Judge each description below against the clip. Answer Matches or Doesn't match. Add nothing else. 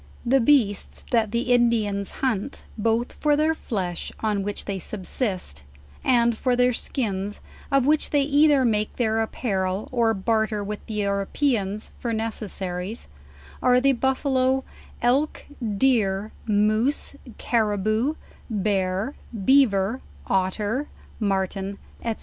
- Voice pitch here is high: Matches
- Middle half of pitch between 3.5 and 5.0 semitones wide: Matches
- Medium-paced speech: Doesn't match